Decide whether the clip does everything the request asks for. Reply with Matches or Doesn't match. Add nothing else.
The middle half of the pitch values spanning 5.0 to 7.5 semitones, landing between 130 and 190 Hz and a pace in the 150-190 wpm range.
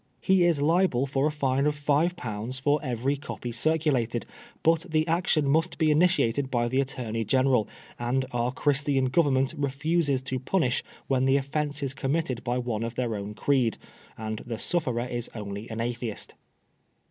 Doesn't match